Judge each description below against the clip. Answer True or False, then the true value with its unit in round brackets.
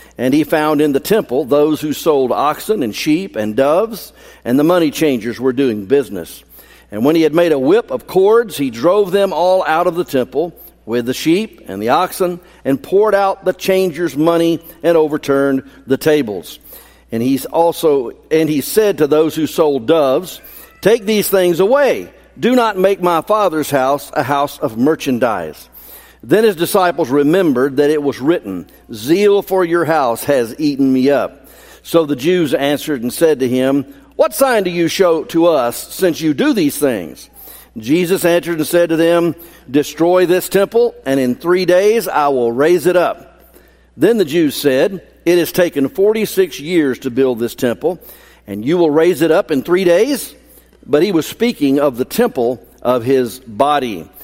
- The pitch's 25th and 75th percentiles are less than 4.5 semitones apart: False (4.8 semitones)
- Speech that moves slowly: False (185 wpm)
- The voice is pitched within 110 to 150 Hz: False (165 Hz)